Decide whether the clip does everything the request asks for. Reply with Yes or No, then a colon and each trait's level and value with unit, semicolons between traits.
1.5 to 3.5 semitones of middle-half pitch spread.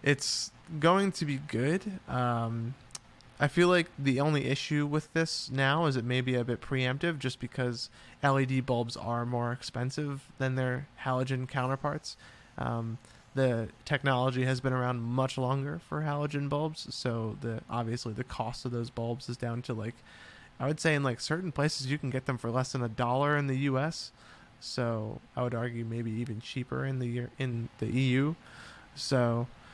Yes: average, 3.0 semitones